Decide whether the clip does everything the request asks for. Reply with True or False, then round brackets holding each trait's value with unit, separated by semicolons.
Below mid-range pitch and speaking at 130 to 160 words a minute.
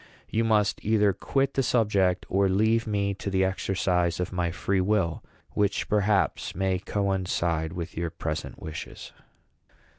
True (95 Hz; 145 wpm)